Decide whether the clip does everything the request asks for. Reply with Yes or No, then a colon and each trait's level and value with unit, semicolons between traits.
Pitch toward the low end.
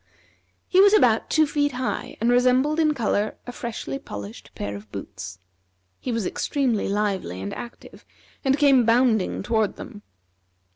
No: high, 235 Hz